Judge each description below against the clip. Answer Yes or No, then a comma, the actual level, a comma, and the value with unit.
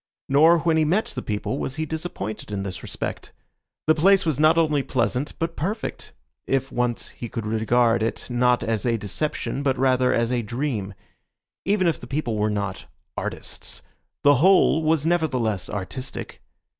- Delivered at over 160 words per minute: Yes, average, 170 wpm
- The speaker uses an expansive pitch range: Yes, wide, 5.7 semitones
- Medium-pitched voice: No, low, 130 Hz